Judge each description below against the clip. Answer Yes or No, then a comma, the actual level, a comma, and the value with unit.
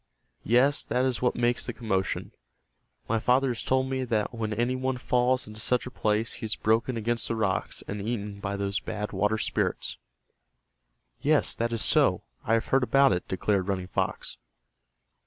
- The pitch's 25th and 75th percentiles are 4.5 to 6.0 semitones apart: No, average, 3.1 semitones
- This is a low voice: Yes, low, 115 Hz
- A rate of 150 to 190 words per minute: Yes, average, 180 wpm